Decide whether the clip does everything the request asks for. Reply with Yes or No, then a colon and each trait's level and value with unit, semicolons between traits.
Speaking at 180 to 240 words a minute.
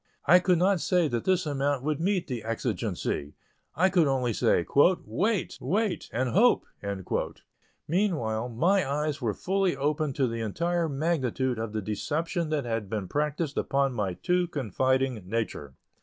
No: average, 155 wpm